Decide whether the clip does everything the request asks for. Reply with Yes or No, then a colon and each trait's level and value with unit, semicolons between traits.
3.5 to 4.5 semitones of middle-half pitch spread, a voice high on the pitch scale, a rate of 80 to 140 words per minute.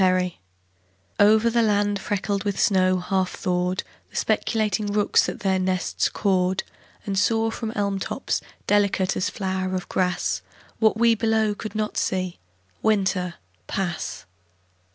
No: narrow, 2.4 semitones; high, 195 Hz; slow, 135 wpm